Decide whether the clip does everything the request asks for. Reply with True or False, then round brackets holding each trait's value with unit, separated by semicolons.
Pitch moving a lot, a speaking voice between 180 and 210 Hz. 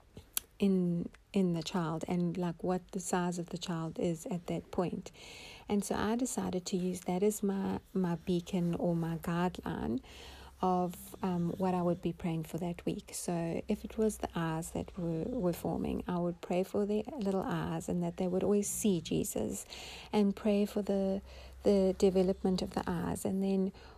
False (2.4 semitones; 185 Hz)